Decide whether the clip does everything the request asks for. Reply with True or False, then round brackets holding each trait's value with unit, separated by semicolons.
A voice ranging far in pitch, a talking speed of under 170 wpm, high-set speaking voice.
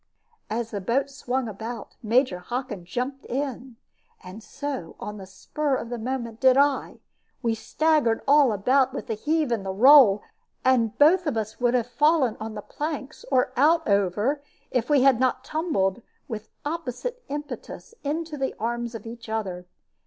False (4.3 semitones; 160 wpm; 250 Hz)